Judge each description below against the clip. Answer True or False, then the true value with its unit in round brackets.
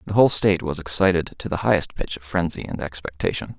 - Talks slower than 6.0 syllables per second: False (6.5 syllables/s)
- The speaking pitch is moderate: False (85 Hz)